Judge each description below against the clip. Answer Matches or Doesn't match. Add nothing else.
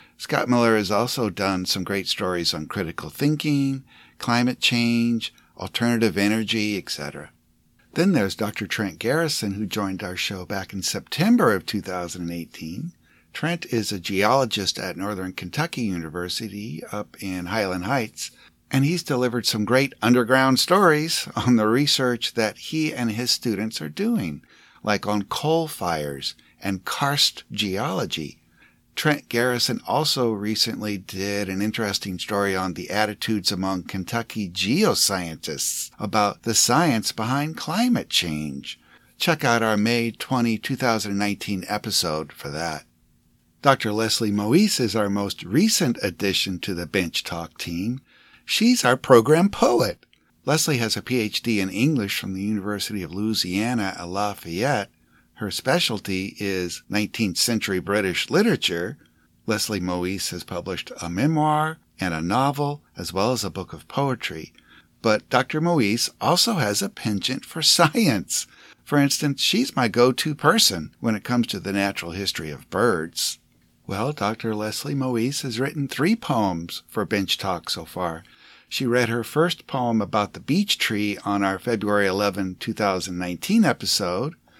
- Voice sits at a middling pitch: Doesn't match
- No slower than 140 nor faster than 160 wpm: Matches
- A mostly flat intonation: Doesn't match